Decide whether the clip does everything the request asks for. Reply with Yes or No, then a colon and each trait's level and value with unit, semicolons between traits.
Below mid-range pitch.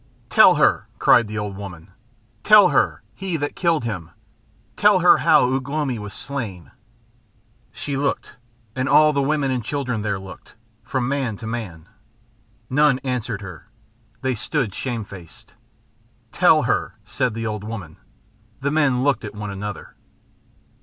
Yes: low, 120 Hz